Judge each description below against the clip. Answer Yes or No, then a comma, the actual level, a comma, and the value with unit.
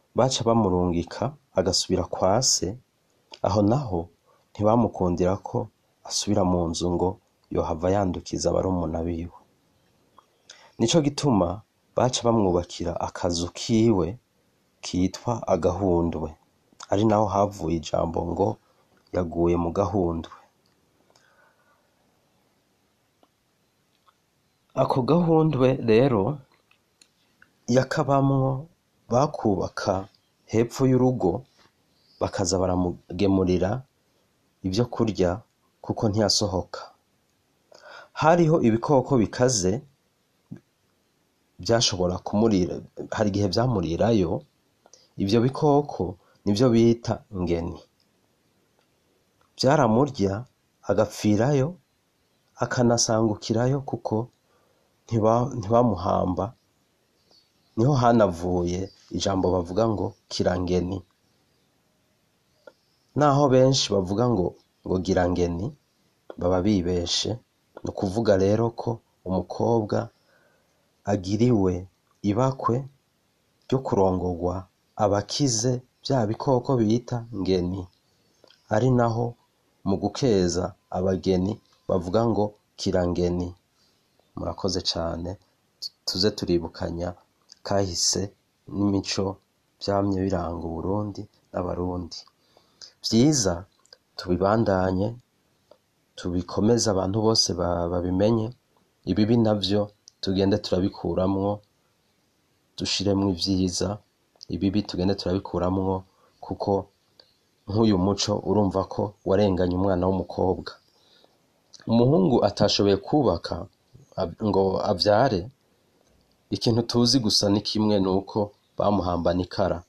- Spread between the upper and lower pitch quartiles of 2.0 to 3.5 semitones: No, average, 4.1 semitones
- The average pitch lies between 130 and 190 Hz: No, low, 100 Hz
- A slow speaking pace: Yes, slow, 75 wpm